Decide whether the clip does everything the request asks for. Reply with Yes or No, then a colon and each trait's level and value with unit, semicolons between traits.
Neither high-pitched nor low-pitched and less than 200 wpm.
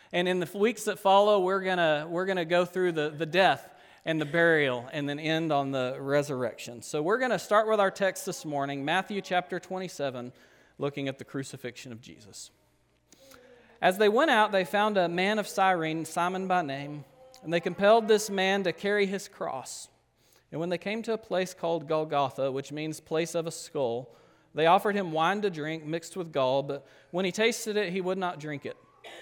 No: medium, 175 Hz; fast, 205 wpm